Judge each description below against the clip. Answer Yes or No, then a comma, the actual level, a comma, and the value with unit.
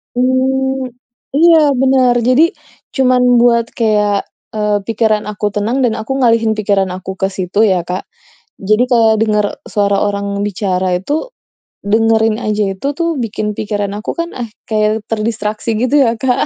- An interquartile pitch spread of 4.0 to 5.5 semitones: No, average, 3.2 semitones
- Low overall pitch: No, high, 220 Hz